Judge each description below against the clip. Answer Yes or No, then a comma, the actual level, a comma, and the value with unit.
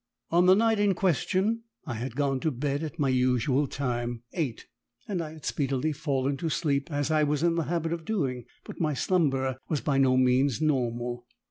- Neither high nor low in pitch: Yes, medium, 145 Hz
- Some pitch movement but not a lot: Yes, average, 4.1 semitones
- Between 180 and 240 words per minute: Yes, average, 200 wpm